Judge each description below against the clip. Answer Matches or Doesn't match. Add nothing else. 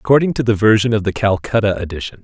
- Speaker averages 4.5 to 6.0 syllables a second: Doesn't match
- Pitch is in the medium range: Doesn't match